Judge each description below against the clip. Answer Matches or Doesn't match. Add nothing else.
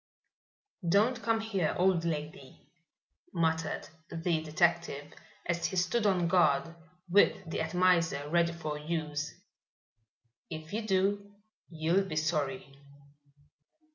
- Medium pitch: Matches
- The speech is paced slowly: Matches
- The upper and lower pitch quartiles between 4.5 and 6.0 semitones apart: Doesn't match